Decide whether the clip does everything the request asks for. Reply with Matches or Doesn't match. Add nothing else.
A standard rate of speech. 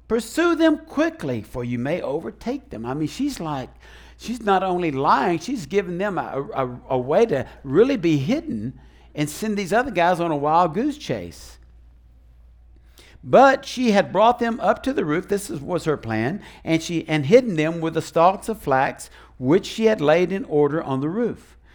Matches